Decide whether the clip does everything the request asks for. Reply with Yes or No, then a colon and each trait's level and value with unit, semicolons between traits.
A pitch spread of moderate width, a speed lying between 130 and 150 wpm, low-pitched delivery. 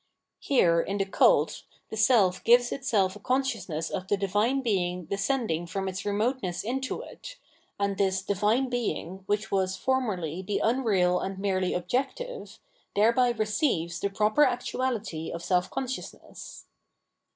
No: average, 4.8 semitones; average, 140 wpm; high, 205 Hz